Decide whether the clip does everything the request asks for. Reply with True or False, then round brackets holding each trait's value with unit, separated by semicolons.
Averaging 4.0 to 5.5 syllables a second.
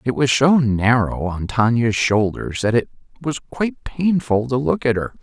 True (4.6 syllables/s)